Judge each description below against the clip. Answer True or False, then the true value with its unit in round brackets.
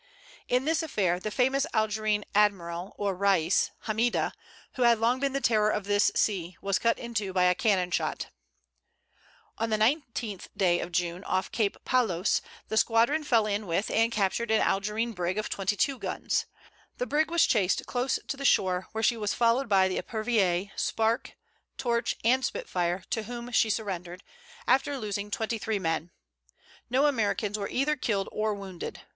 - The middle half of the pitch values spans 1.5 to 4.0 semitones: True (3.6 semitones)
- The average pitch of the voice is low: False (215 Hz)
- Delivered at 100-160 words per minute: False (175 wpm)